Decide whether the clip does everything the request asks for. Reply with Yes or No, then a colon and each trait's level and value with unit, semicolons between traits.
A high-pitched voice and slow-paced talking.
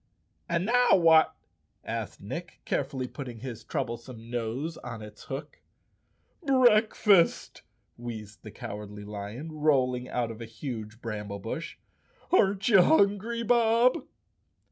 No: low, 130 Hz; slow, 125 wpm